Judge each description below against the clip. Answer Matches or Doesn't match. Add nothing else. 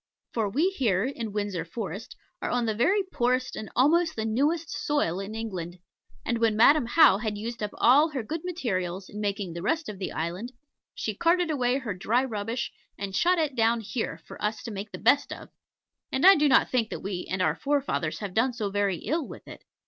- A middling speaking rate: Doesn't match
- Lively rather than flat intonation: Matches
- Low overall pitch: Doesn't match